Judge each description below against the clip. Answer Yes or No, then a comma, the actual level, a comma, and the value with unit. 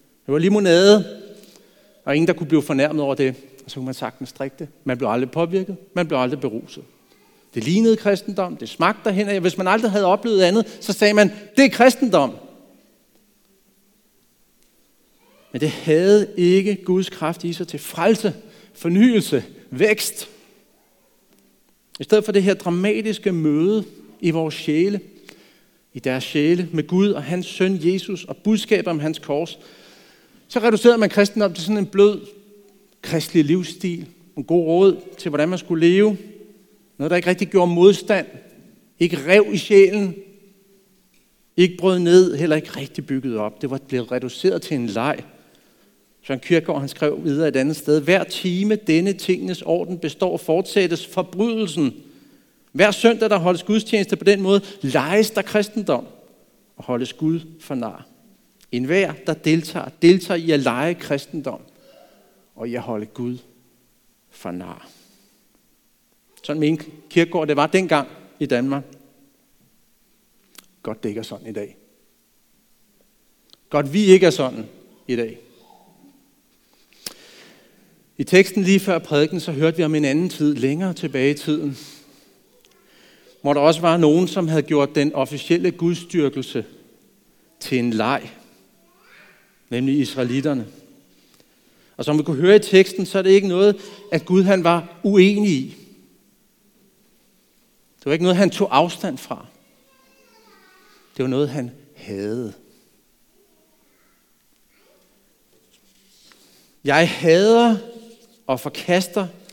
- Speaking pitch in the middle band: Yes, medium, 180 Hz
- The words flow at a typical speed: No, slow, 140 wpm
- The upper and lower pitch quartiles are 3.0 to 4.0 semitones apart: No, average, 5.2 semitones